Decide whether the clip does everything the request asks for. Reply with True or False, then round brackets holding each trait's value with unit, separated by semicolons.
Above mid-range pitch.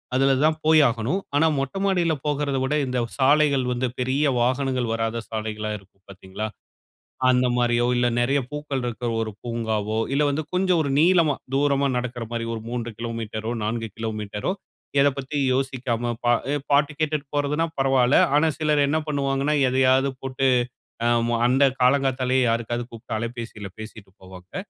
False (130 Hz)